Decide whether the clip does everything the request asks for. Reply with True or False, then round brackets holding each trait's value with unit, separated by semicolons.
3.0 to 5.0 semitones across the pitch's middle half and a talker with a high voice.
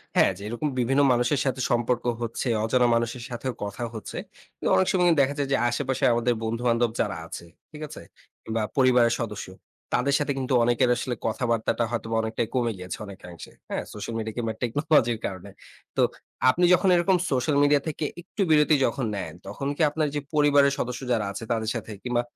False (3.7 semitones; 120 Hz)